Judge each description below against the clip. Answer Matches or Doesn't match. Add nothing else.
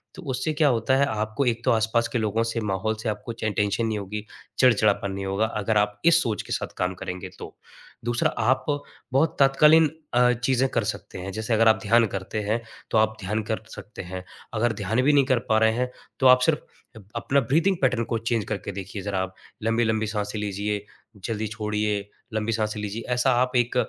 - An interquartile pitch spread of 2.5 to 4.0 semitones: Matches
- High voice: Doesn't match